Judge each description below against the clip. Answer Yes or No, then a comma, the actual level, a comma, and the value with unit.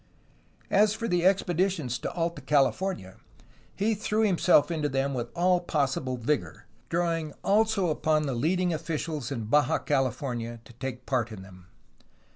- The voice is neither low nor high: Yes, medium, 150 Hz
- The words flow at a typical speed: Yes, average, 145 wpm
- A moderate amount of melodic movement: No, wide, 5.8 semitones